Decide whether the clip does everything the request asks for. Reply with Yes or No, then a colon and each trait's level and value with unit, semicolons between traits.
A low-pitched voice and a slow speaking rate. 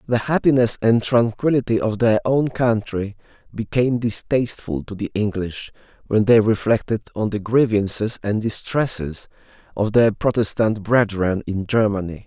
Yes: low, 110 Hz; slow, 130 wpm